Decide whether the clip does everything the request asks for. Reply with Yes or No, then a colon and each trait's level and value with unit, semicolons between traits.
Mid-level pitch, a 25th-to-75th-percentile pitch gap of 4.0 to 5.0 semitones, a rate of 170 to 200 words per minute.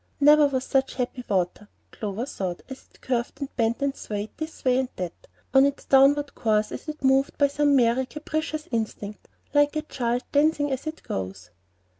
No: very high, 265 Hz; average, 4.3 semitones; average, 185 wpm